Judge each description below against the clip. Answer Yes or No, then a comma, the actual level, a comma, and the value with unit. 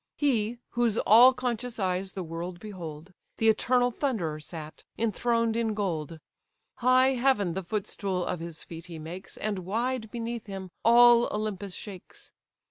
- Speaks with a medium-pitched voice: No, high, 210 Hz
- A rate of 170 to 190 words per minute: No, average, 145 wpm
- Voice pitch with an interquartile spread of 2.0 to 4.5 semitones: No, average, 4.9 semitones